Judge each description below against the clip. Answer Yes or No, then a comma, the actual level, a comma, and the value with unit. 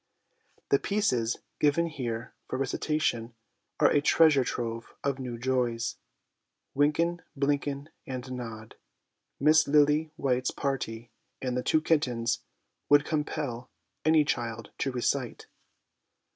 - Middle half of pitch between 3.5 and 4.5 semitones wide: Yes, average, 3.8 semitones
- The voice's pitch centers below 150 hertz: Yes, low, 135 Hz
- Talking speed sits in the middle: No, slow, 120 wpm